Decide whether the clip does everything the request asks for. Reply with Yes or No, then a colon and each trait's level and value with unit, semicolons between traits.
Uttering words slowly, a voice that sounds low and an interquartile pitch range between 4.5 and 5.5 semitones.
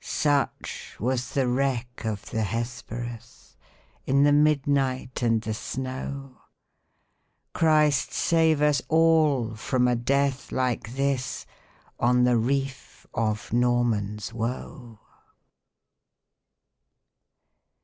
No: slow, 95 wpm; low, 125 Hz; average, 2.9 semitones